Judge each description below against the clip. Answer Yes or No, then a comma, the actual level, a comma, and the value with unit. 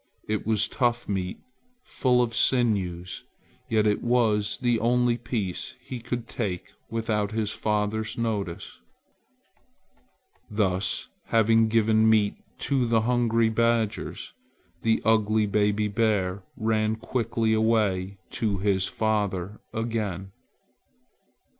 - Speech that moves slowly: Yes, slow, 110 wpm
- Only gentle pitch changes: Yes, narrow, 2.0 semitones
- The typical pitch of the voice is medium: No, low, 110 Hz